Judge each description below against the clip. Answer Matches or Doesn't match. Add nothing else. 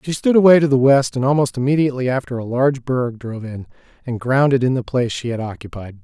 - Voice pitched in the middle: Doesn't match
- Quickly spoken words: Matches